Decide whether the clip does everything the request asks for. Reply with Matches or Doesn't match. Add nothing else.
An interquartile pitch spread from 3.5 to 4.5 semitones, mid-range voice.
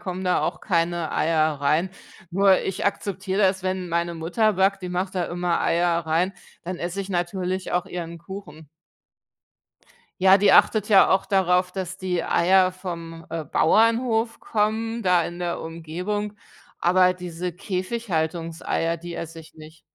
Doesn't match